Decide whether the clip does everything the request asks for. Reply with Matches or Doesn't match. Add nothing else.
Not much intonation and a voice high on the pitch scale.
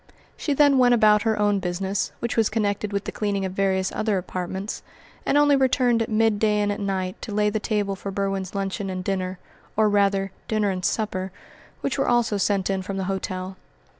Matches